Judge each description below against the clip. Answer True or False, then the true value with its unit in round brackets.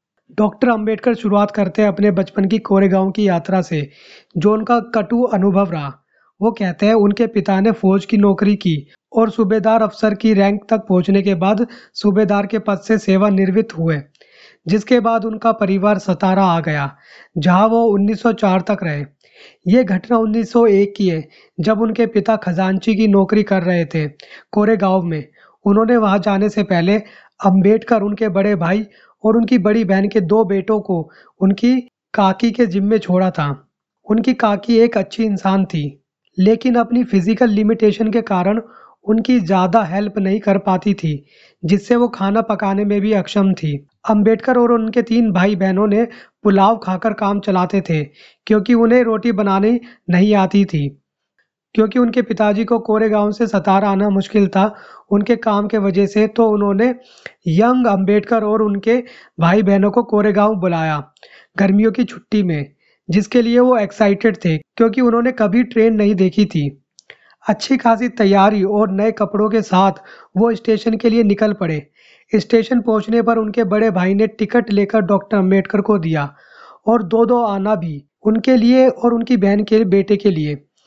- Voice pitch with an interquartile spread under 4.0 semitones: True (2.6 semitones)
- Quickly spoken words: False (165 wpm)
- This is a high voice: True (210 Hz)